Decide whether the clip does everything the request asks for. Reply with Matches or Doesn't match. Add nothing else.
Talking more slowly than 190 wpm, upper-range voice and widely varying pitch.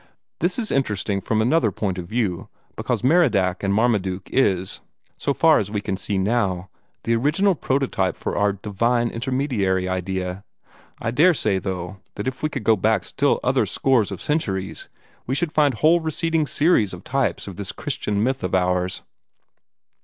Doesn't match